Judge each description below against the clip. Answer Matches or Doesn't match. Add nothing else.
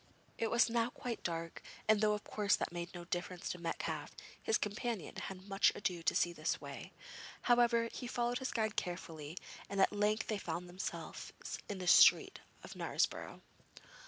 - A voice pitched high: Matches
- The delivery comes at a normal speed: Matches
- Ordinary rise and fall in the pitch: Matches